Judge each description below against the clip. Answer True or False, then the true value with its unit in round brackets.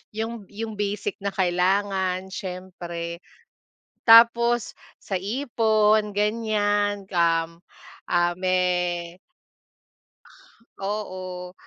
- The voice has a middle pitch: False (195 Hz)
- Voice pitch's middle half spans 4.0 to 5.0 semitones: False (2.9 semitones)